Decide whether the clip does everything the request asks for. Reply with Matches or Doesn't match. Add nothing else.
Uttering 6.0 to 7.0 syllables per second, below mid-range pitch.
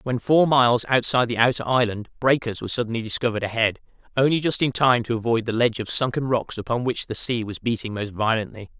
Matches